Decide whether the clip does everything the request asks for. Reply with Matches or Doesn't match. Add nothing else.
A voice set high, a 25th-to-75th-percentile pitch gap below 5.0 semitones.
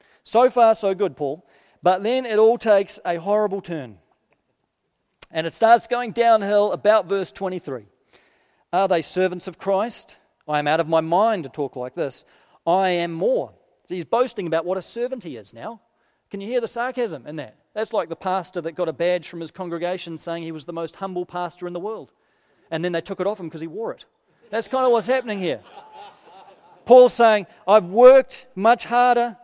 Doesn't match